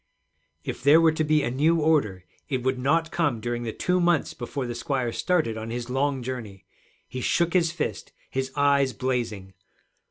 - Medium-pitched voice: No, low, 130 Hz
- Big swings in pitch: No, average, 4.6 semitones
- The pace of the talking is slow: No, average, 185 wpm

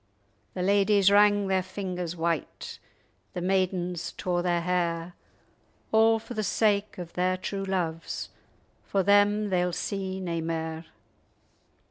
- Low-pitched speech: No, medium, 185 Hz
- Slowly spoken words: Yes, slow, 125 wpm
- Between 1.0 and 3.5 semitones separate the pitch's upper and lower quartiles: Yes, narrow, 2.5 semitones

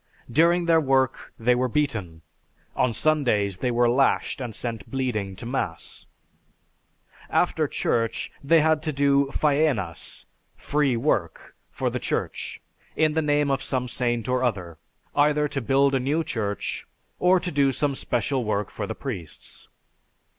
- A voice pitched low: Yes, low, 130 Hz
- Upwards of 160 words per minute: No, average, 145 wpm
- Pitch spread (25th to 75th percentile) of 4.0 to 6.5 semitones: Yes, average, 4.4 semitones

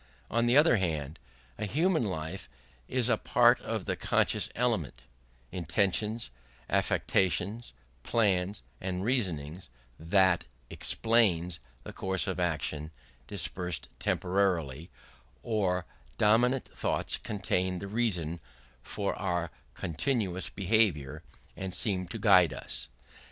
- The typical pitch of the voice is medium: No, very low, 95 Hz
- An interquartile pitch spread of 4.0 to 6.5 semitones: Yes, average, 4.3 semitones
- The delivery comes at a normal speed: No, slow, 110 wpm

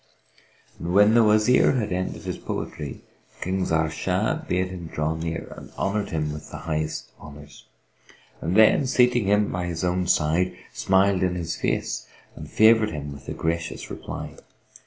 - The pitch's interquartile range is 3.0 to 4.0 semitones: No, average, 4.4 semitones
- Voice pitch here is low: Yes, very low, 90 Hz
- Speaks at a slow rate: No, average, 155 wpm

